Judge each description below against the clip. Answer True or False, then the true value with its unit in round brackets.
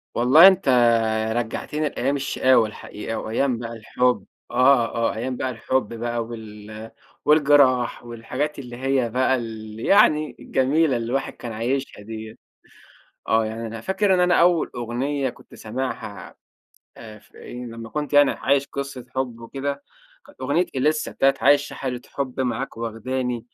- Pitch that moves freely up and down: False (3.3 semitones)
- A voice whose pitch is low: True (125 Hz)